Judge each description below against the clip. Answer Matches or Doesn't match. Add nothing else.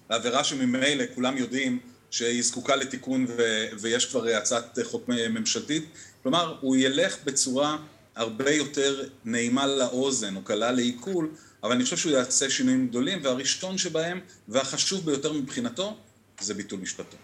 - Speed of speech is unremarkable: Matches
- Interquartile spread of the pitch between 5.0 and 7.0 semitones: Matches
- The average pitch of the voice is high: Doesn't match